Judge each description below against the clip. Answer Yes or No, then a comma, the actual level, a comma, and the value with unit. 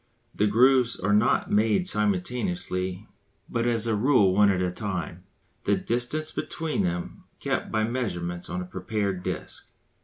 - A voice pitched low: Yes, low, 105 Hz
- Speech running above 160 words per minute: No, average, 155 wpm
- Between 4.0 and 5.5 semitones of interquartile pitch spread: Yes, average, 4.5 semitones